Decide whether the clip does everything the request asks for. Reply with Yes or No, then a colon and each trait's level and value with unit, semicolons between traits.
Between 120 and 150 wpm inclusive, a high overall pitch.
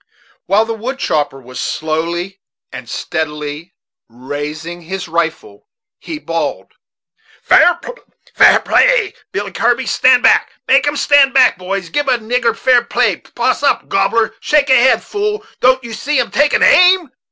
Yes: average, 145 wpm; high, 225 Hz